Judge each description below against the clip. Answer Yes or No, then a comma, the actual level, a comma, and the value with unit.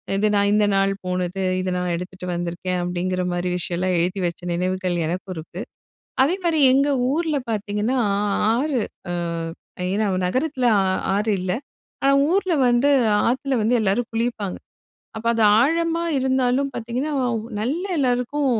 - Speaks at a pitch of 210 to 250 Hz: Yes, high, 220 Hz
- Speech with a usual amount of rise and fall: No, wide, 6.7 semitones